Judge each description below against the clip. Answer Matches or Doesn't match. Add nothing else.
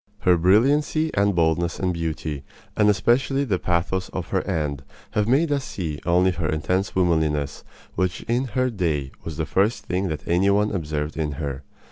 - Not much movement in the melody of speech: Doesn't match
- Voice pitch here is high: Doesn't match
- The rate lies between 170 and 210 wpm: Matches